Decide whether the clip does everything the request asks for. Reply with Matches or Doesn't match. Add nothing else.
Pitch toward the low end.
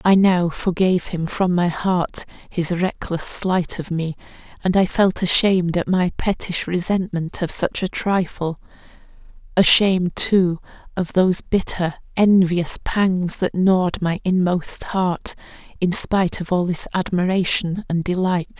Doesn't match